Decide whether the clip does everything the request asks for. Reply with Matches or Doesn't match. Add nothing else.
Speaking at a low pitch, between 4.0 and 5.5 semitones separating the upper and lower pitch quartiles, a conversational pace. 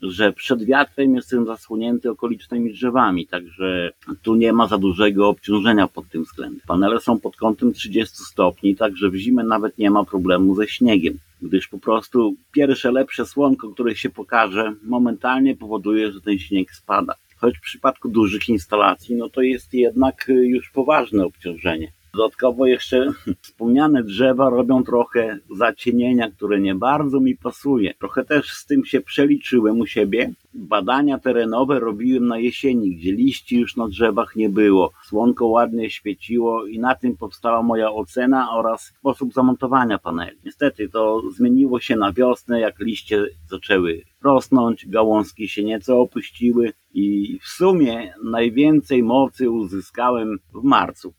Doesn't match